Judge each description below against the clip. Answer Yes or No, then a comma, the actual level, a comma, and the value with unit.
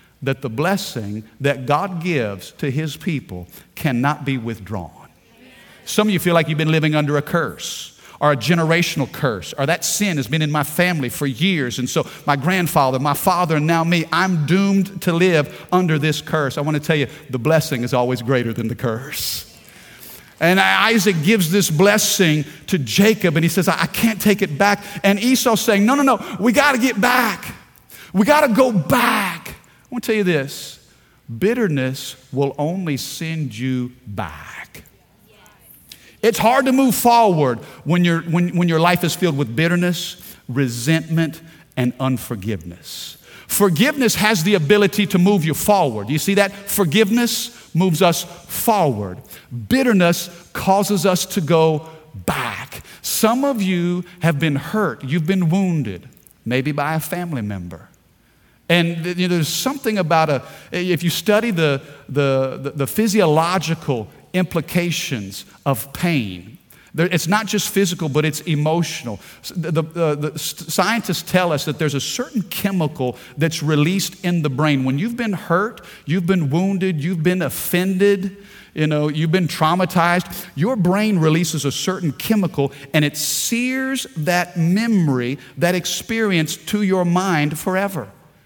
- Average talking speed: Yes, average, 155 wpm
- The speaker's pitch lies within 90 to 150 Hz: No, medium, 165 Hz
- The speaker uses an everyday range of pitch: Yes, average, 4.9 semitones